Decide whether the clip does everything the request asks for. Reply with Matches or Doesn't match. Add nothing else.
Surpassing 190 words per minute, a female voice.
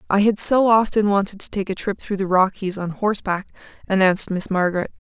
Matches